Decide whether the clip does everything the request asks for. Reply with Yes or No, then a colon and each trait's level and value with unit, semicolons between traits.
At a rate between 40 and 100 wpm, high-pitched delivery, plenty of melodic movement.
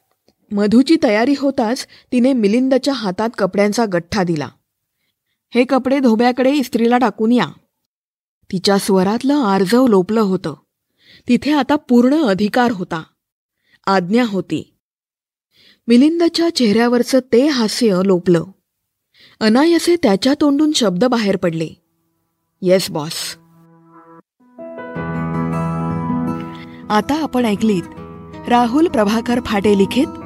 Yes: average, 95 wpm; high, 220 Hz; wide, 6.2 semitones